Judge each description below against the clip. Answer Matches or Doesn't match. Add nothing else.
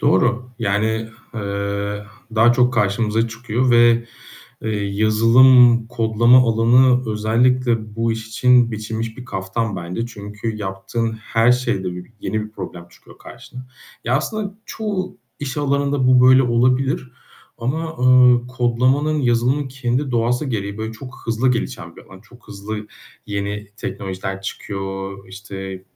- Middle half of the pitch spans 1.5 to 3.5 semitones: Matches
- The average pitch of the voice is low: Matches